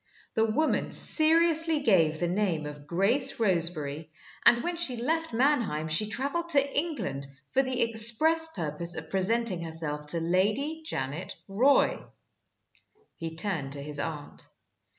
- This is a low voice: No, high, 210 Hz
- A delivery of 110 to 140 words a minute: Yes, slow, 135 wpm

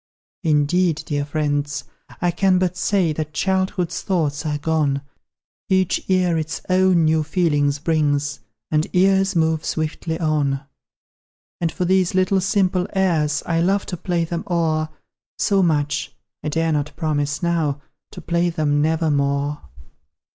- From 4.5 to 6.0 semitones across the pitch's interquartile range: No, average, 3.5 semitones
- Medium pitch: Yes, medium, 160 Hz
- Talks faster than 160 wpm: No, average, 140 wpm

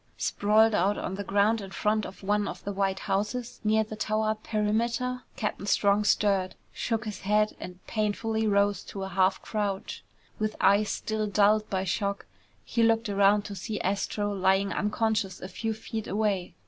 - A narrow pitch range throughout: Yes, narrow, 1.6 semitones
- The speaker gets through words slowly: No, average, 170 wpm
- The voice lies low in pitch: No, high, 210 Hz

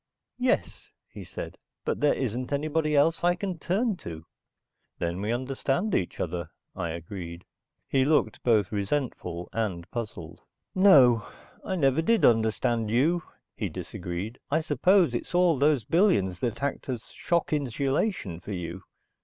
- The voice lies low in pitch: Yes, low, 125 Hz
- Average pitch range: No, wide, 8.5 semitones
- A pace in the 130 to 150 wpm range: Yes, average, 145 wpm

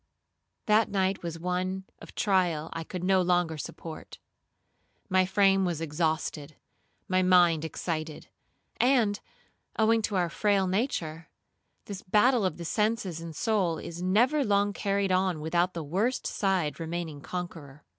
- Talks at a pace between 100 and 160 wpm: Yes, average, 140 wpm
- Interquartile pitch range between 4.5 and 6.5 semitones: No, average, 3.4 semitones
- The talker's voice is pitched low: No, medium, 185 Hz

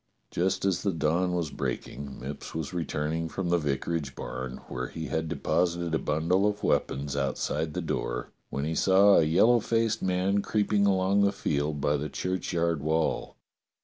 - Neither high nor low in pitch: No, very low, 80 Hz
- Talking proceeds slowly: No, average, 170 wpm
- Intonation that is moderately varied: Yes, average, 4.1 semitones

